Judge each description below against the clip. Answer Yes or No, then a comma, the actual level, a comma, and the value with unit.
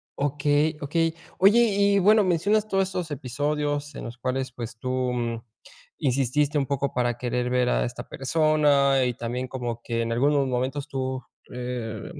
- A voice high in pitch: No, low, 135 Hz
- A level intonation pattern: No, average, 3.3 semitones